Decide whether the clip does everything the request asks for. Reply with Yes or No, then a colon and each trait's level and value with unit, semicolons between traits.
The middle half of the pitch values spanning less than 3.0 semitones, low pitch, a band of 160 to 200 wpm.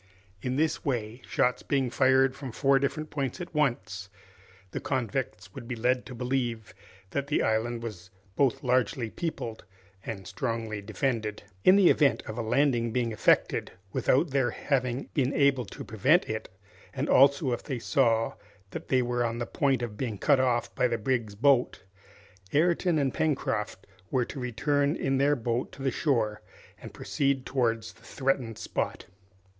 No: average, 3.3 semitones; low, 125 Hz; average, 165 wpm